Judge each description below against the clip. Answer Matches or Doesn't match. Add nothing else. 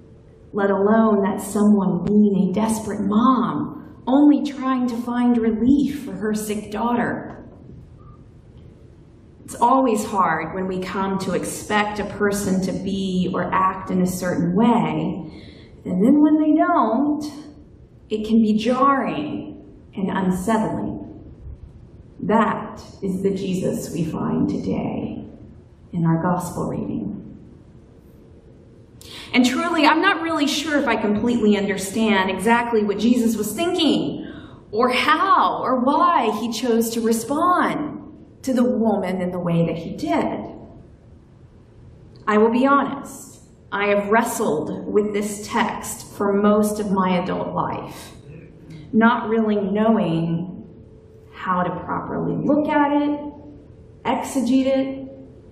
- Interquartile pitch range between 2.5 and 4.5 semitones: Doesn't match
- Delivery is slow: Matches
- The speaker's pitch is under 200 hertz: Doesn't match